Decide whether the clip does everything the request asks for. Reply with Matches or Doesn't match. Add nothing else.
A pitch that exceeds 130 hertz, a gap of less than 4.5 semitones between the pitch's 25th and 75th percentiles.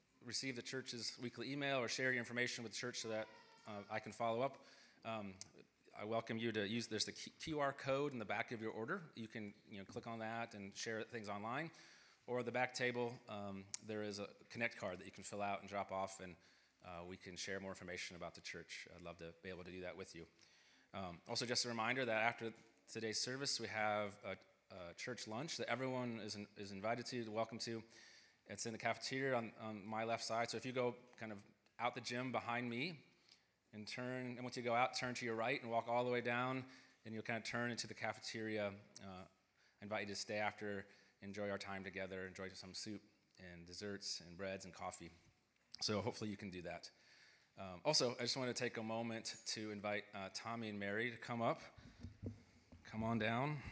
Doesn't match